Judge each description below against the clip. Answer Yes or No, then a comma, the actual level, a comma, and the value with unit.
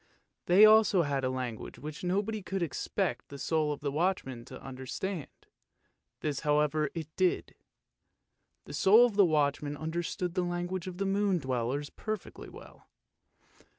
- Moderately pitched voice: Yes, medium, 160 Hz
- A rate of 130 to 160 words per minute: Yes, average, 150 wpm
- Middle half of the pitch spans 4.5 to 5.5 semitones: Yes, average, 4.8 semitones